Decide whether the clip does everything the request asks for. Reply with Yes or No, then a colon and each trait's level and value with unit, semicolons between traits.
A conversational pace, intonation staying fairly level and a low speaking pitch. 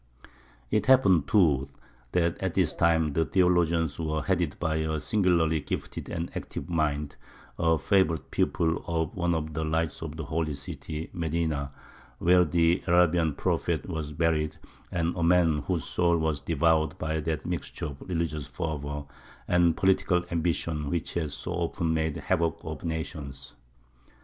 Yes: average, 150 wpm; narrow, 1.9 semitones; very low, 80 Hz